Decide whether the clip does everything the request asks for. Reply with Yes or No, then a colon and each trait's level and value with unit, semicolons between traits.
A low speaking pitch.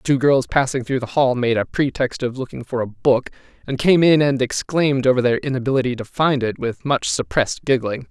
Yes: low, 130 Hz